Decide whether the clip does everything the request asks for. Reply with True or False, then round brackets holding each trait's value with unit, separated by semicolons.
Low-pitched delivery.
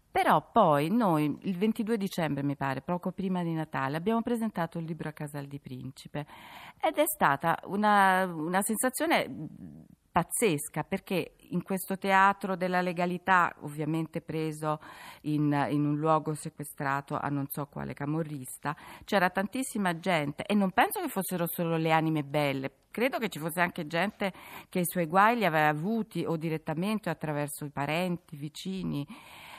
False (170 Hz)